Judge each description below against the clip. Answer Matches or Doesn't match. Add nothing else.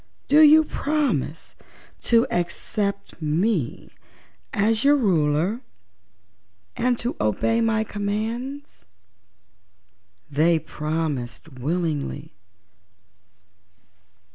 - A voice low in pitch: Doesn't match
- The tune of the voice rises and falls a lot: Matches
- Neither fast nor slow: Doesn't match